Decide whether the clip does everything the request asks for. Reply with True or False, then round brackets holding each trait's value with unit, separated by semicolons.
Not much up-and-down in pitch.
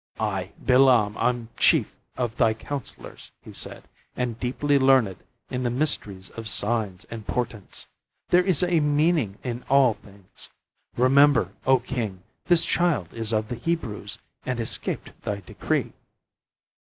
False (4.2 semitones)